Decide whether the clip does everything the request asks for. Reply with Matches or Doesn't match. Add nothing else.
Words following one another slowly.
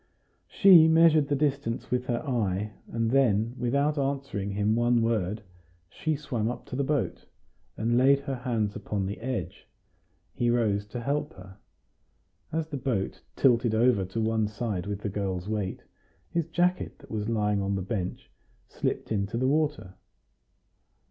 Doesn't match